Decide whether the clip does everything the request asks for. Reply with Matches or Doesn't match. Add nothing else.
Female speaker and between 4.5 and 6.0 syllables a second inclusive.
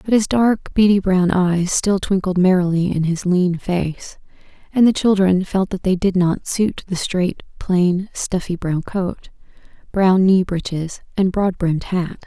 Doesn't match